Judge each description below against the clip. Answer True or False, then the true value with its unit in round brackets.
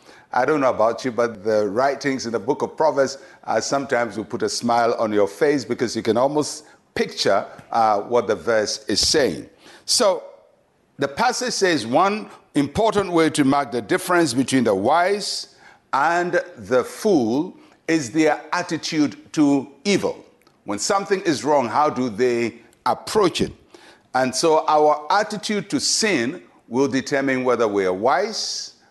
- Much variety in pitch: True (5.8 semitones)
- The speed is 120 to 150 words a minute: False (160 wpm)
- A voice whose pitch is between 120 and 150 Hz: True (140 Hz)